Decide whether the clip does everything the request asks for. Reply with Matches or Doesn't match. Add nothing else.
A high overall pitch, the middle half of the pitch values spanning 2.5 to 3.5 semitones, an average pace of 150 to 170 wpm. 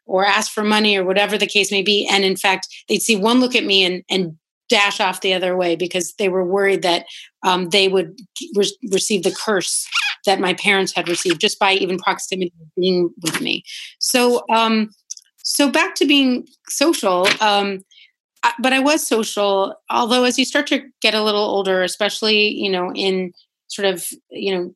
Doesn't match